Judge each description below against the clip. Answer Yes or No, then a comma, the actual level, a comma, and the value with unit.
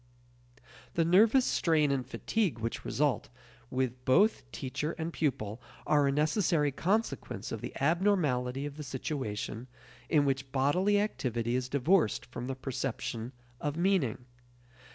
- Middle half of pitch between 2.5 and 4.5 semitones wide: No, average, 4.9 semitones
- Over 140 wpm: No, slow, 135 wpm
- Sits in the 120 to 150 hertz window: Yes, medium, 140 Hz